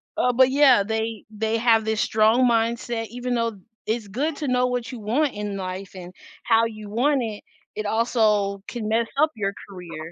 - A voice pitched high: Yes, high, 225 Hz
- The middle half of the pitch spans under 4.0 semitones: Yes, average, 2.9 semitones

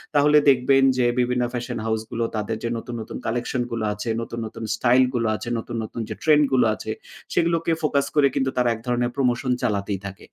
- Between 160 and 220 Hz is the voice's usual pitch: No, low, 120 Hz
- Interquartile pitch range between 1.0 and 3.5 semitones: Yes, average, 2.8 semitones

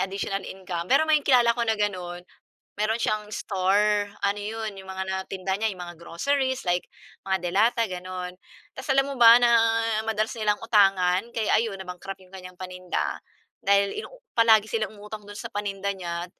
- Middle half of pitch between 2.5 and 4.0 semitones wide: Yes, average, 3.2 semitones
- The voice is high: Yes, high, 200 Hz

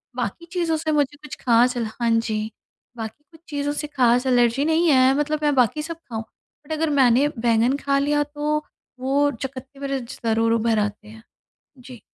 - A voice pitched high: Yes, very high, 265 Hz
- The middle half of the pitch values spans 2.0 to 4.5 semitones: Yes, average, 4.0 semitones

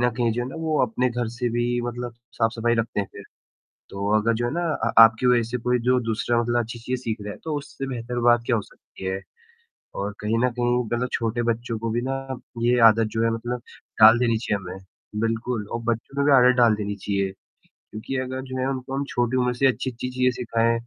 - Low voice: Yes, low, 120 Hz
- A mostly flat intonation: Yes, narrow, 1.8 semitones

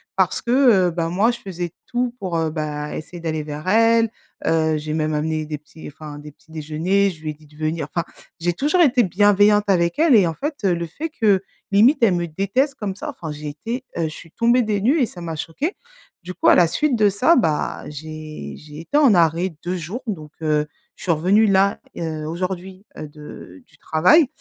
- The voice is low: No, medium, 175 Hz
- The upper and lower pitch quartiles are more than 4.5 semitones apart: Yes, wide, 5.5 semitones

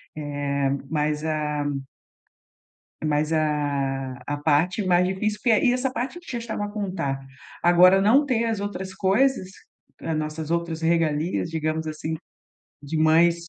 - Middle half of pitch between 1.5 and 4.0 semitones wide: No, average, 5.0 semitones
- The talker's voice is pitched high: No, medium, 165 Hz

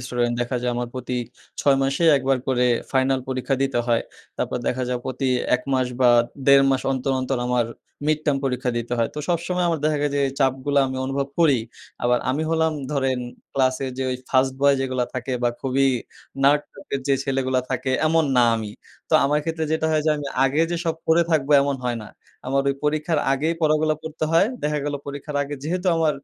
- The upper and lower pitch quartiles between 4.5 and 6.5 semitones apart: No, average, 2.8 semitones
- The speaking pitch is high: No, low, 135 Hz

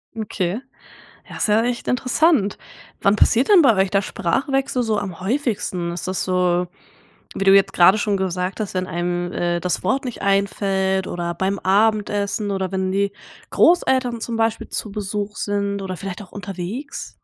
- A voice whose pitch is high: Yes, high, 200 Hz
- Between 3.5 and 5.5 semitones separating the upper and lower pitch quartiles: No, average, 3.0 semitones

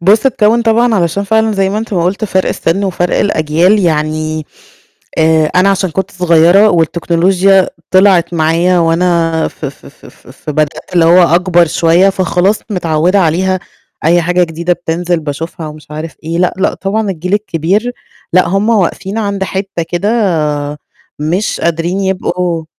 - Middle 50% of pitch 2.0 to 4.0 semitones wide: Yes, average, 3.0 semitones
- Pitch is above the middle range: No, medium, 180 Hz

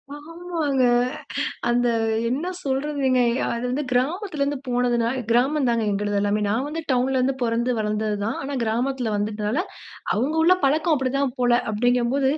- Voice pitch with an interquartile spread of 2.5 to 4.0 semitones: Yes, average, 3.4 semitones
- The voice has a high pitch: Yes, very high, 255 Hz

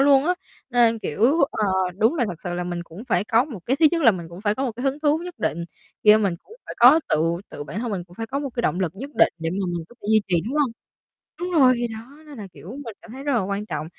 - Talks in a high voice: Yes, high, 225 Hz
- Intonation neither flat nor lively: No, wide, 6.8 semitones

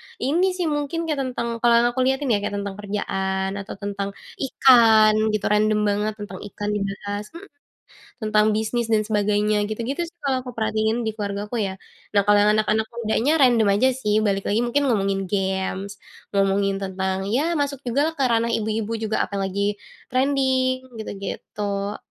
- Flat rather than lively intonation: No, average, 3.8 semitones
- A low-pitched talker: No, high, 215 Hz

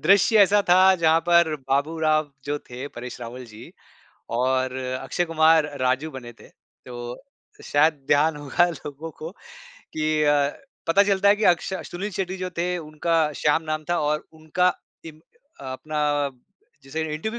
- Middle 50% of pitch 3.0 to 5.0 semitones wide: Yes, average, 3.6 semitones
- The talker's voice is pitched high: No, medium, 155 Hz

